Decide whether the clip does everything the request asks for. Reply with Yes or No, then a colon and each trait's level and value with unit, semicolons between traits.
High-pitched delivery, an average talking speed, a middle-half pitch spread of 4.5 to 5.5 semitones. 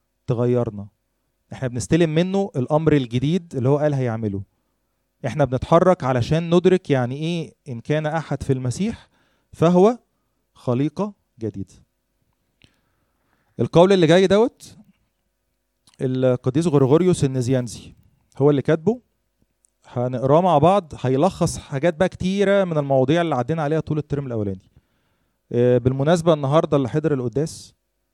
No: medium, 145 Hz; average, 115 wpm; average, 5.1 semitones